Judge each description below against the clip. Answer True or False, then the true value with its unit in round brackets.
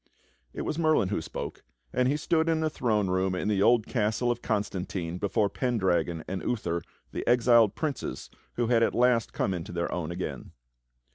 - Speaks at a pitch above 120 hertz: False (110 Hz)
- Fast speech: False (185 wpm)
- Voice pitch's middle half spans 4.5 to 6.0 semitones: True (4.9 semitones)